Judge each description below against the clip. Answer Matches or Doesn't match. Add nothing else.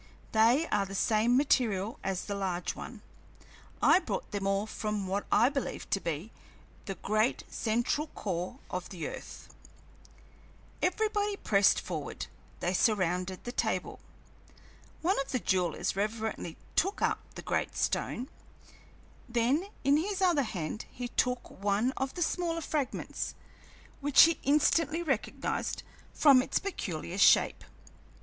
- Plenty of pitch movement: Matches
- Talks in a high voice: Matches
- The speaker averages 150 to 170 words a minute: Doesn't match